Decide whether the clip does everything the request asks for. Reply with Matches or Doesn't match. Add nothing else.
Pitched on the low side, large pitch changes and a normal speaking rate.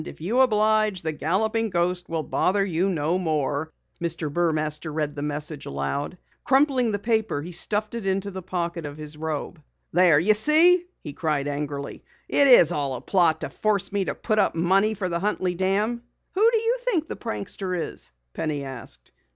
Doesn't match